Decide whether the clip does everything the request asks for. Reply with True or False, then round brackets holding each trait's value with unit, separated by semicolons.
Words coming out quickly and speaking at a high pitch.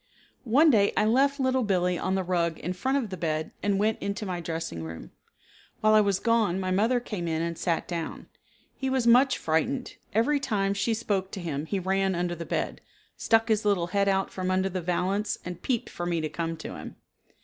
True (215 wpm; 195 Hz)